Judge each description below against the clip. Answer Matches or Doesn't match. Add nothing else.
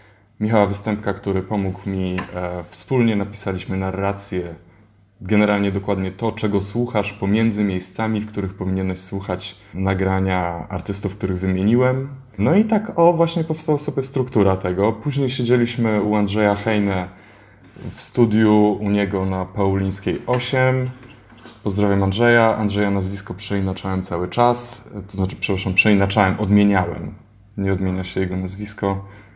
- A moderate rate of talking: Matches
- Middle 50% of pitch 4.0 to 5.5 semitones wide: Doesn't match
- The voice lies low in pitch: Matches